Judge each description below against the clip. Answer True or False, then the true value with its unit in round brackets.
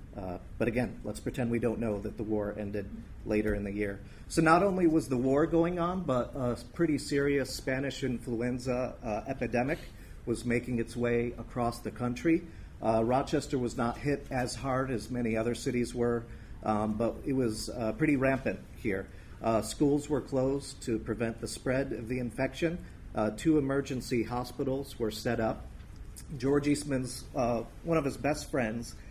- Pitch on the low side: True (120 Hz)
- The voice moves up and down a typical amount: True (3.6 semitones)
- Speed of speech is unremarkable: True (175 wpm)